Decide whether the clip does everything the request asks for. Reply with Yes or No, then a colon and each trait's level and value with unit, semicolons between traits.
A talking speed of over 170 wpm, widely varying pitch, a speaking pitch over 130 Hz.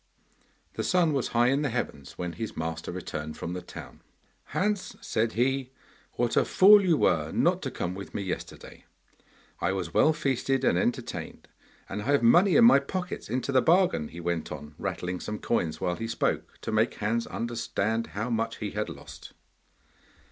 No: average, 185 wpm; wide, 7.3 semitones; low, 115 Hz